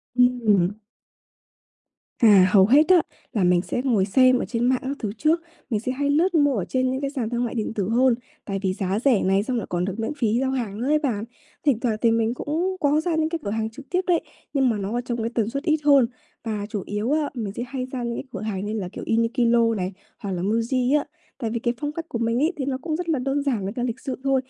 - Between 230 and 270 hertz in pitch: Yes, high, 240 Hz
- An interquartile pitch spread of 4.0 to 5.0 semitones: Yes, average, 4.3 semitones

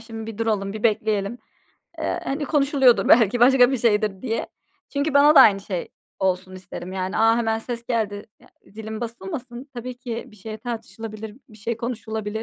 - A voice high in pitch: Yes, high, 225 Hz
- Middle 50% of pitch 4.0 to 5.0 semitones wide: No, average, 2.7 semitones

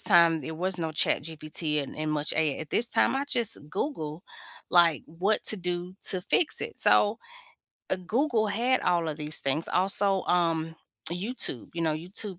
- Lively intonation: No, average, 4.4 semitones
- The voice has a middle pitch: Yes, medium, 175 Hz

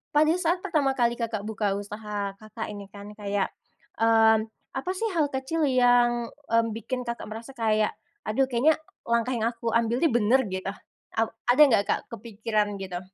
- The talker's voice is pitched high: Yes, high, 230 Hz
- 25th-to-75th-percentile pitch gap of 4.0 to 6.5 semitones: No, average, 3.3 semitones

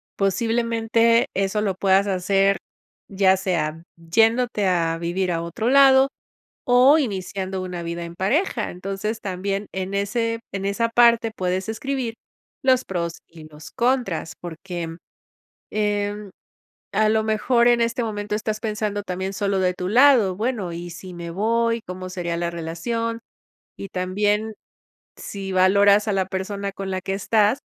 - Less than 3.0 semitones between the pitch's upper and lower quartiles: No, average, 3.6 semitones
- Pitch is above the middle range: Yes, high, 200 Hz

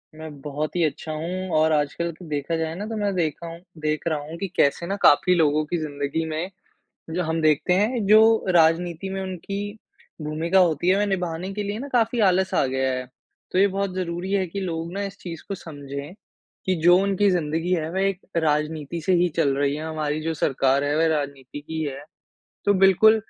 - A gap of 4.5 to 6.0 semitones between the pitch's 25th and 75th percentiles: No, average, 3.7 semitones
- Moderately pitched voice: Yes, medium, 165 Hz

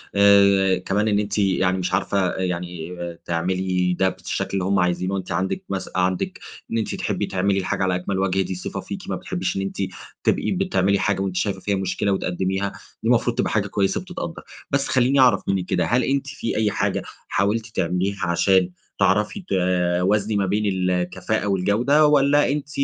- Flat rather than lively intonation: Yes, narrow, 2.0 semitones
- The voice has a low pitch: Yes, very low, 95 Hz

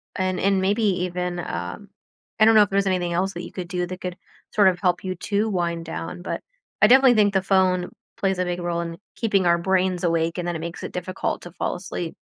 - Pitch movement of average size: No, narrow, 1.9 semitones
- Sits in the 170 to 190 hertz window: Yes, medium, 185 Hz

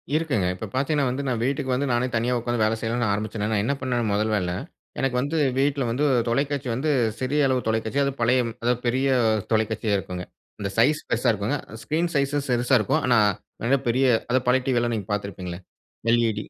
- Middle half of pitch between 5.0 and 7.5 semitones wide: No, average, 3.6 semitones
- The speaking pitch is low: Yes, low, 125 Hz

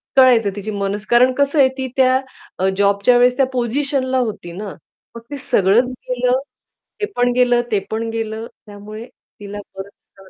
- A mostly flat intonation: No, average, 3.8 semitones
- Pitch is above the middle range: Yes, high, 230 Hz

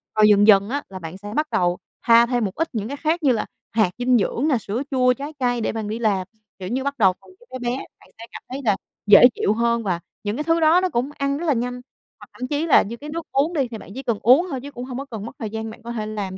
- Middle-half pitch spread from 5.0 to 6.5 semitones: No, average, 4.6 semitones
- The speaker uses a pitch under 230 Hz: No, high, 240 Hz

